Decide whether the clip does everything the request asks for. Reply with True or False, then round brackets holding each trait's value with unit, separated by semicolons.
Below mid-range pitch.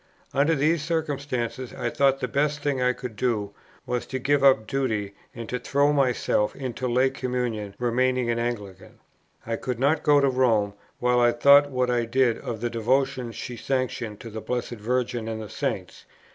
True (125 Hz)